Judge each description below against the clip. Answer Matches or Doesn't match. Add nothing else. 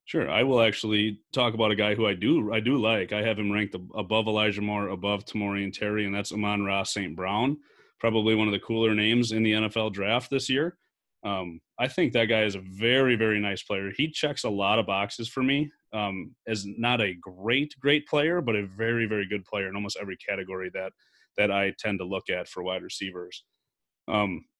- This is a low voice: Matches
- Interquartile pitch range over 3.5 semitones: Doesn't match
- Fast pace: Matches